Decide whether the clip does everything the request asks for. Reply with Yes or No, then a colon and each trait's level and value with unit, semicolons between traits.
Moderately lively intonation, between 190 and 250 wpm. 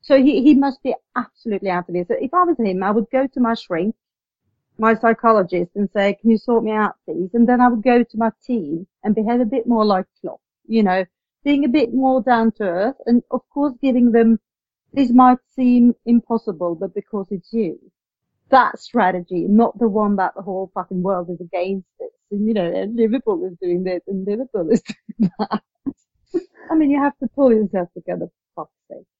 Yes: average, 4.1 semitones; fast, 205 wpm